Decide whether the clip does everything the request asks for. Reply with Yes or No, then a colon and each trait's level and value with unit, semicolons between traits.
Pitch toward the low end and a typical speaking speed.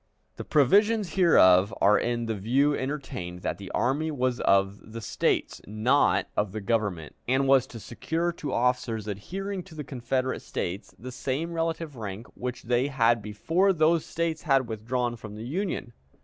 Yes: low, 125 Hz; average, 165 wpm